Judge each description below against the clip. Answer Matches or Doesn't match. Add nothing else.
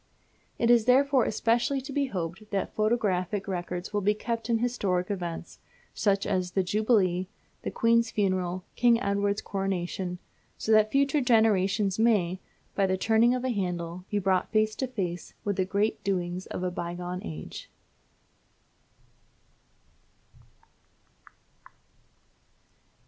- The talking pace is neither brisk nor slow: Doesn't match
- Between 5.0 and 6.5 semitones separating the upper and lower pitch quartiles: Doesn't match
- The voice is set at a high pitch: Matches